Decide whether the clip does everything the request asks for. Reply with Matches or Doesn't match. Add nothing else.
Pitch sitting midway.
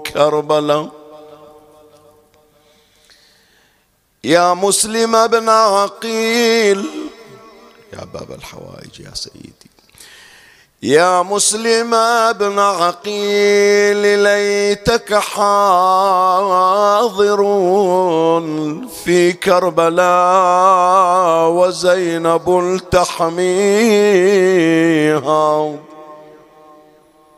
Matches